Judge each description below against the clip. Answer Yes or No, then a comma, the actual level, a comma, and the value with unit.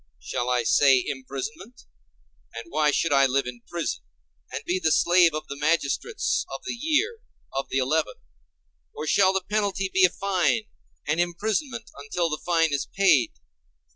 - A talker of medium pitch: Yes, medium, 165 Hz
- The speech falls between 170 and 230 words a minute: No, average, 160 wpm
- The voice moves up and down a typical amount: No, wide, 5.8 semitones